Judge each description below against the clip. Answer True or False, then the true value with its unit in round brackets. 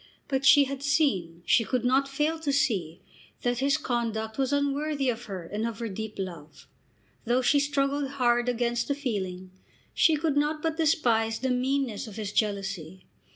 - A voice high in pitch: True (245 Hz)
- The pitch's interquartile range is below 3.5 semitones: False (4.7 semitones)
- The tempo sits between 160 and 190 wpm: True (175 wpm)